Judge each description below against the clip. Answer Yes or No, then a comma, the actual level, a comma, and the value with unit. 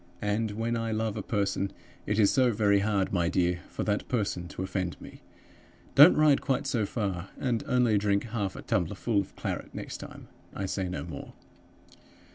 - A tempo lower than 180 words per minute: No, average, 185 wpm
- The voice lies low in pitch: Yes, low, 105 Hz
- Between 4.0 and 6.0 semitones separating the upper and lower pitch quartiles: No, average, 2.7 semitones